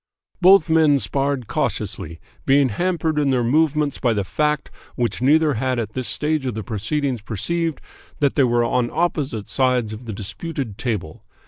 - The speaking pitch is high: No, low, 135 Hz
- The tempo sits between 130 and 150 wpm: No, average, 165 wpm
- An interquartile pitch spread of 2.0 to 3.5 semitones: No, average, 4.6 semitones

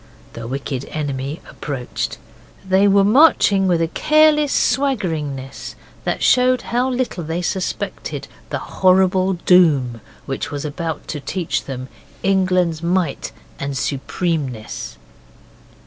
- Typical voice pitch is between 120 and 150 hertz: No, medium, 175 Hz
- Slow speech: Yes, slow, 115 wpm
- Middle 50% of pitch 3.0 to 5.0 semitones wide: No, wide, 5.6 semitones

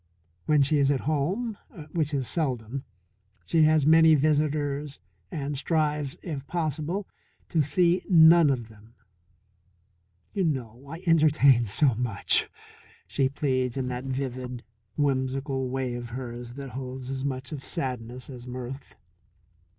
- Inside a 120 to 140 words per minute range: Yes, slow, 135 wpm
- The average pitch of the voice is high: No, medium, 140 Hz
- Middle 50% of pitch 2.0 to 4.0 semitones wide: Yes, average, 3.3 semitones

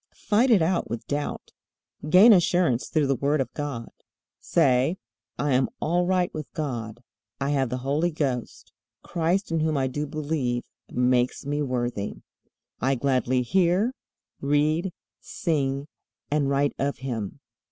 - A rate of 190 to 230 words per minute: No, average, 140 wpm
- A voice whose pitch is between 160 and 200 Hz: No, medium, 145 Hz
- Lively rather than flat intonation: No, average, 4.1 semitones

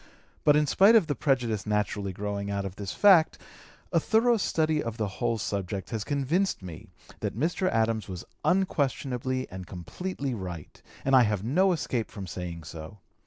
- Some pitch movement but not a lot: No, wide, 7.3 semitones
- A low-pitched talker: Yes, low, 115 Hz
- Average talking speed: Yes, average, 170 wpm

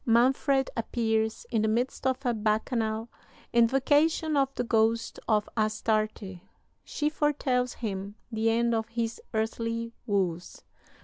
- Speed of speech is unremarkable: No, slow, 125 wpm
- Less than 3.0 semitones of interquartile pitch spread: Yes, narrow, 2.4 semitones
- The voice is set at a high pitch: Yes, high, 230 Hz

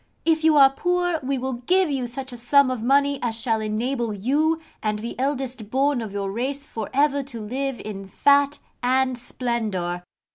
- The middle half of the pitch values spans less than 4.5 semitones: Yes, average, 3.9 semitones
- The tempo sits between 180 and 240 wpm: Yes, average, 185 wpm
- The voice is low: No, very high, 255 Hz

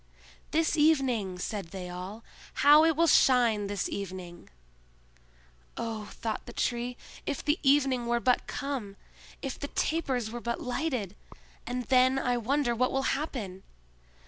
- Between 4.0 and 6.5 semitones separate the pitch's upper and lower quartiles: Yes, average, 4.6 semitones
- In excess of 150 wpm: No, average, 145 wpm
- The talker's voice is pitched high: Yes, high, 245 Hz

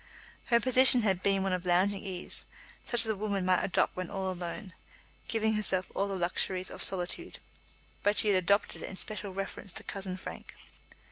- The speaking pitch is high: Yes, high, 195 Hz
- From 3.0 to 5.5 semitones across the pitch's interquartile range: No, narrow, 2.4 semitones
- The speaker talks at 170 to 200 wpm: Yes, average, 190 wpm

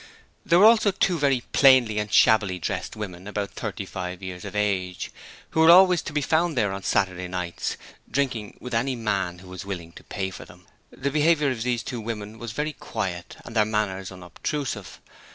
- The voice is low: Yes, low, 105 Hz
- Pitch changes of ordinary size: No, wide, 6.5 semitones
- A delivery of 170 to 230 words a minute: Yes, average, 195 wpm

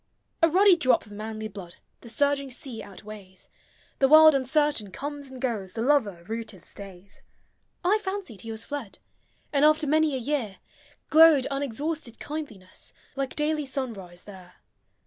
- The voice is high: Yes, very high, 260 Hz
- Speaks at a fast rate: No, average, 150 wpm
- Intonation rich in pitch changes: Yes, wide, 6.0 semitones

